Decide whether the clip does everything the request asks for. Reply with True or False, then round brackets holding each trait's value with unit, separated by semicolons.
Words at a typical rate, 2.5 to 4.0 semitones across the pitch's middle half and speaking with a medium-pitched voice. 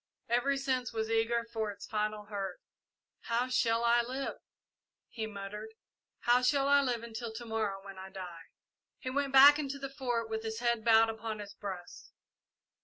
False (175 wpm; 2.8 semitones; 230 Hz)